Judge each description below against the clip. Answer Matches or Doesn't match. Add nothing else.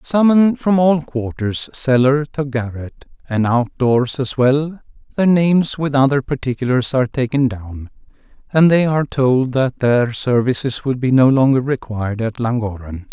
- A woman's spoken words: Doesn't match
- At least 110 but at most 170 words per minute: Matches